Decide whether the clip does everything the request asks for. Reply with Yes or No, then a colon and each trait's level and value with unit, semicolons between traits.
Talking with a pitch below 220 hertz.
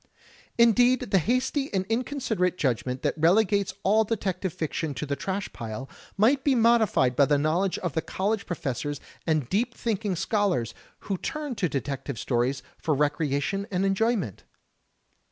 Yes: high, 190 Hz